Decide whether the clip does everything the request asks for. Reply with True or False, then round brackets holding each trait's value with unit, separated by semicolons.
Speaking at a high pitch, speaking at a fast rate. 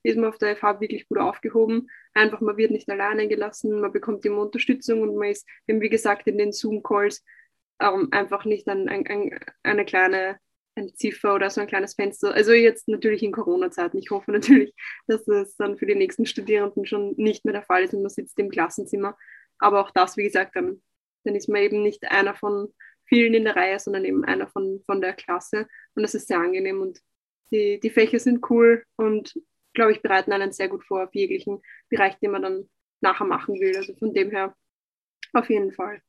True (215 Hz; 210 wpm)